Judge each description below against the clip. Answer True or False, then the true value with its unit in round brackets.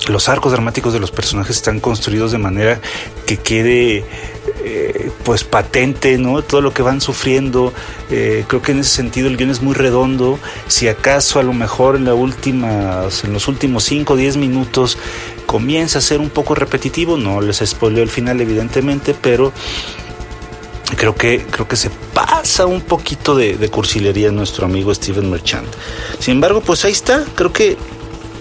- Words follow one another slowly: False (175 wpm)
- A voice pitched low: True (125 Hz)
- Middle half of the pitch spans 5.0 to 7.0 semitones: False (3.9 semitones)